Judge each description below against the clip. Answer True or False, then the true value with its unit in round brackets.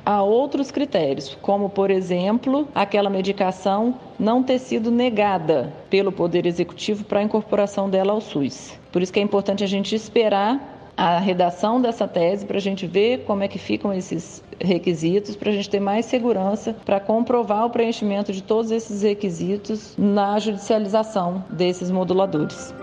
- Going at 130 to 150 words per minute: False (160 wpm)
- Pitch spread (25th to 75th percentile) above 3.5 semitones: False (2.4 semitones)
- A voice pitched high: True (205 Hz)